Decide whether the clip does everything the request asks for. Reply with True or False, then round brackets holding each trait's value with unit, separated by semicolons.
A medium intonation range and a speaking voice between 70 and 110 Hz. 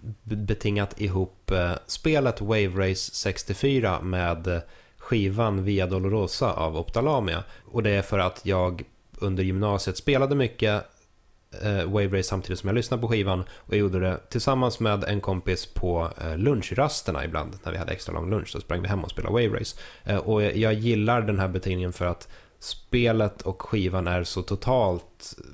True (3.2 semitones; 100 Hz)